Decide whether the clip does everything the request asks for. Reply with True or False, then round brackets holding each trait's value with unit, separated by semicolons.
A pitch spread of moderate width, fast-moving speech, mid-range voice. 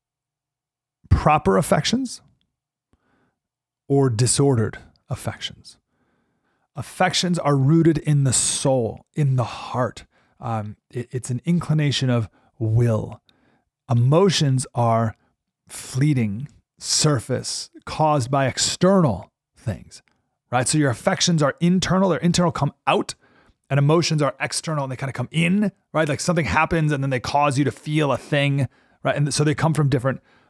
False (3.8 semitones; 135 wpm; 145 Hz)